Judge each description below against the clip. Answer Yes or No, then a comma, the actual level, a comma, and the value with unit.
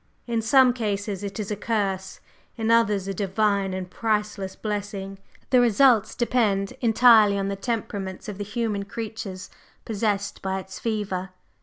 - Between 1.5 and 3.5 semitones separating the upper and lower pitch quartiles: Yes, narrow, 2.4 semitones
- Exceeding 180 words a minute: No, average, 150 wpm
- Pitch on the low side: No, high, 205 Hz